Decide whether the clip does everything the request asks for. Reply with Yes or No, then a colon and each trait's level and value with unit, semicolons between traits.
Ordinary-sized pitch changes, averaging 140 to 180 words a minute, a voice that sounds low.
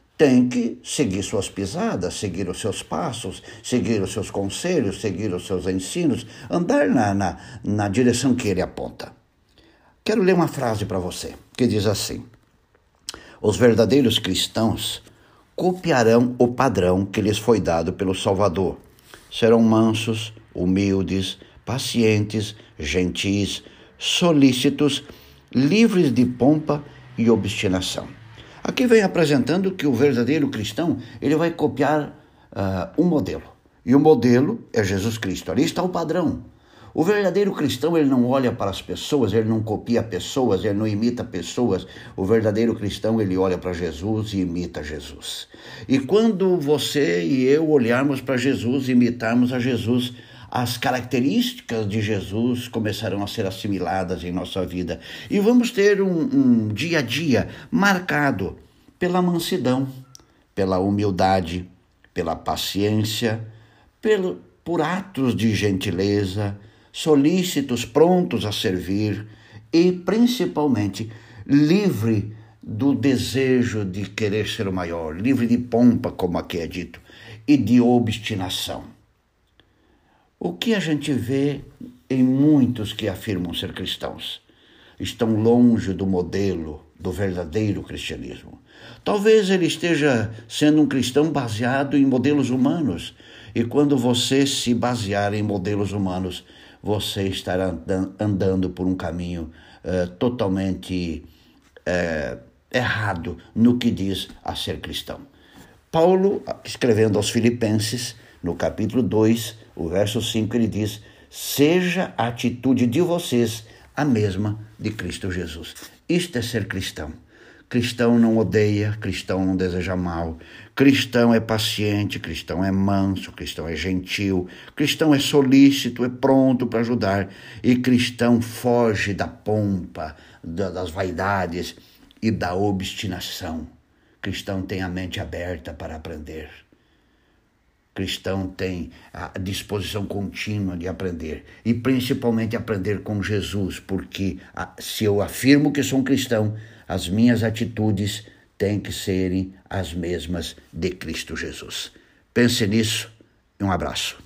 No: average, 4.9 semitones; average, 130 wpm; low, 110 Hz